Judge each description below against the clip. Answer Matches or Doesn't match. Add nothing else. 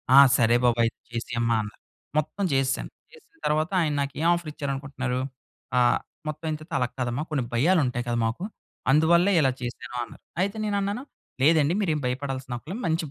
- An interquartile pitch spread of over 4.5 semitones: Matches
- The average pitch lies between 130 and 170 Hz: Matches